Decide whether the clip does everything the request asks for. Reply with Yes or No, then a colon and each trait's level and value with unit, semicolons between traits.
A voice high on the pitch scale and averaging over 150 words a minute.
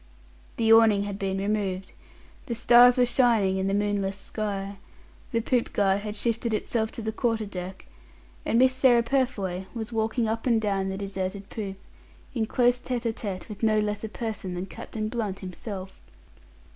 Yes: high, 215 Hz; average, 175 wpm